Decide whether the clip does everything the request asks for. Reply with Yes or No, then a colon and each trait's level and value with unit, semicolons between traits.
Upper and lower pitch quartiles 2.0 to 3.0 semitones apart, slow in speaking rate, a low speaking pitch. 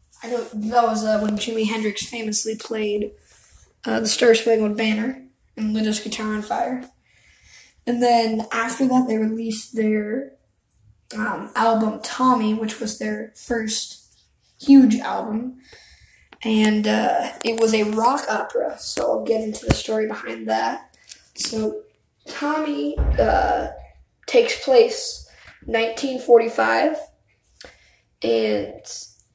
No: narrow, 2.4 semitones; slow, 125 wpm; high, 225 Hz